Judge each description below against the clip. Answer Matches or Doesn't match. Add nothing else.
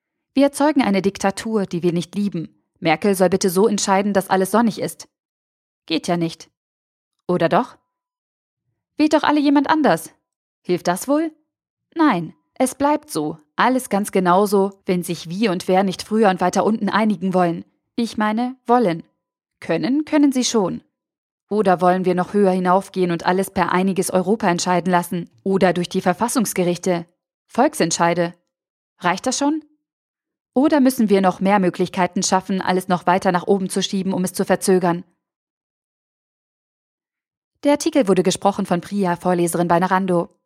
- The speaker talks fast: Doesn't match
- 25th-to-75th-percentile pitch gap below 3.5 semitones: Doesn't match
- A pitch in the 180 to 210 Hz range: Matches